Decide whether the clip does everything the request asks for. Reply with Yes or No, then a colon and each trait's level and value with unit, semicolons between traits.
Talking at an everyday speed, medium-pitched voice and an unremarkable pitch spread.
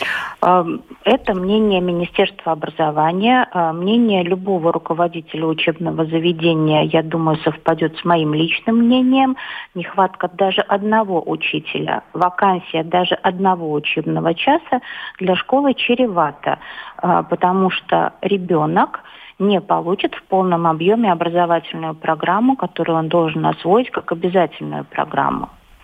No: slow, 105 wpm; medium, 175 Hz; average, 3.6 semitones